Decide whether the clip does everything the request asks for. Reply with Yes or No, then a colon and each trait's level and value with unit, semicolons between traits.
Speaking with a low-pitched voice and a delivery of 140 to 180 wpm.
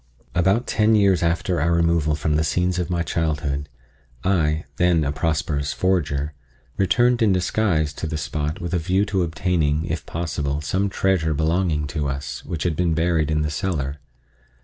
Yes: very low, 80 Hz; average, 170 wpm